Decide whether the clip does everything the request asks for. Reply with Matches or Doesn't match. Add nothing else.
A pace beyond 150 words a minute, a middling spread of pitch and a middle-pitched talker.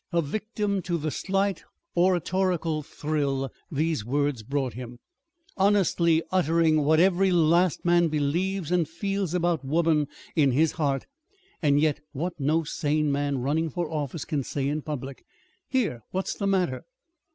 Doesn't match